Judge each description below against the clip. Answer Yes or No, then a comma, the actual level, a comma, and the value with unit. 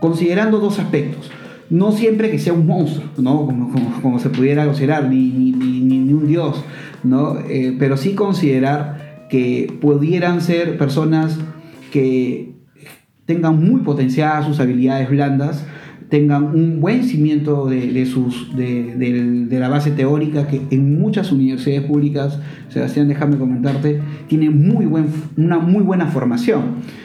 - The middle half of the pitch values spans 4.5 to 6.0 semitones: No, average, 3.2 semitones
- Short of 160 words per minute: Yes, average, 145 wpm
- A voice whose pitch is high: No, medium, 145 Hz